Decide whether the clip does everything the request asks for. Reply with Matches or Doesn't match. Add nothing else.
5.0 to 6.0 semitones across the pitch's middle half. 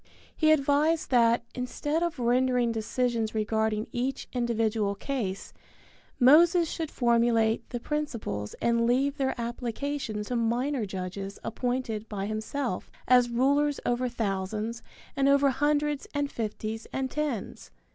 Doesn't match